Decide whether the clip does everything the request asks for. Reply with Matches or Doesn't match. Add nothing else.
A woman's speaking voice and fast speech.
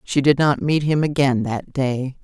Matches